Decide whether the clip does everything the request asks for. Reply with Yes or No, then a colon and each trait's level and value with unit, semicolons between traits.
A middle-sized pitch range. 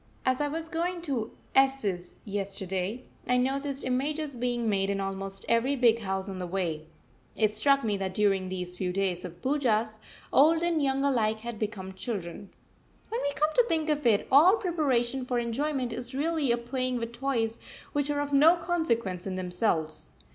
No: wide, 6.3 semitones